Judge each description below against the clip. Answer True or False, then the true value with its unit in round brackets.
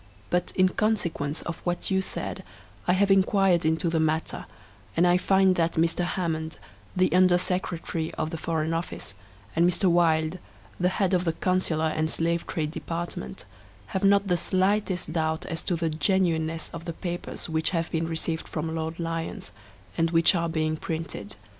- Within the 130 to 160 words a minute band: False (170 wpm)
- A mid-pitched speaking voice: True (170 Hz)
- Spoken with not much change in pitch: True (2.2 semitones)